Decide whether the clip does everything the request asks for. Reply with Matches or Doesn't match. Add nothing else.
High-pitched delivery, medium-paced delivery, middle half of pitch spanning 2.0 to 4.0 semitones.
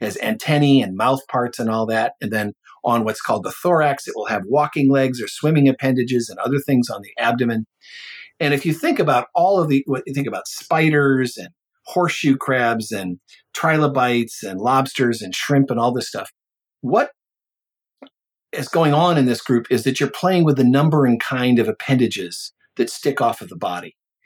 Doesn't match